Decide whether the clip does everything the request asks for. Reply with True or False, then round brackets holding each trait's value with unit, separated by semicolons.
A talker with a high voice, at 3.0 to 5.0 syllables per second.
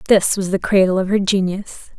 False (195 Hz; 5.2 syllables/s)